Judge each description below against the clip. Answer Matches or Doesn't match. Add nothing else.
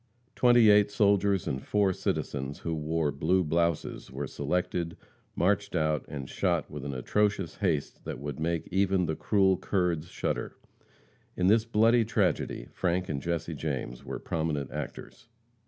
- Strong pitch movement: Doesn't match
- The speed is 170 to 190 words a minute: Doesn't match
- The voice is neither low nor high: Doesn't match